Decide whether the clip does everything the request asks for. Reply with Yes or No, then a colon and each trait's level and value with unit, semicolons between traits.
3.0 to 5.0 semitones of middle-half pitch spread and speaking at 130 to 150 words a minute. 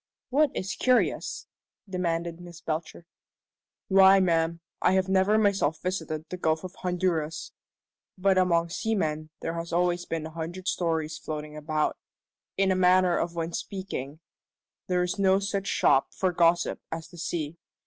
No: narrow, 2.6 semitones; average, 145 wpm